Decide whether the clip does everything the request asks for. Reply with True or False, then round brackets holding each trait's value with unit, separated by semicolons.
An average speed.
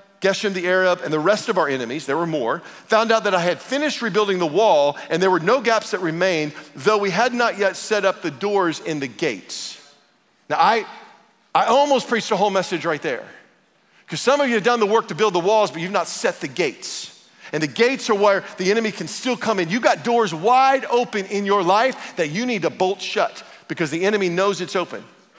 False (235 wpm)